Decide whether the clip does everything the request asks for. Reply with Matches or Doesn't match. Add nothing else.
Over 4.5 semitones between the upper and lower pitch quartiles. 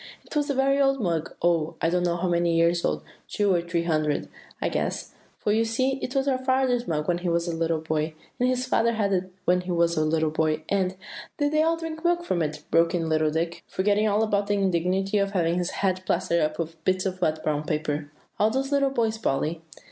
Matches